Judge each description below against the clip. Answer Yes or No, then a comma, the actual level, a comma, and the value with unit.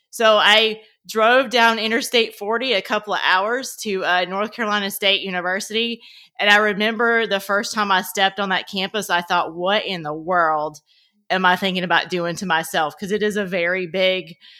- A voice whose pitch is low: No, high, 195 Hz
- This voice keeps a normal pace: Yes, average, 190 wpm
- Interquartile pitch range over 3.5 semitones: No, average, 2.9 semitones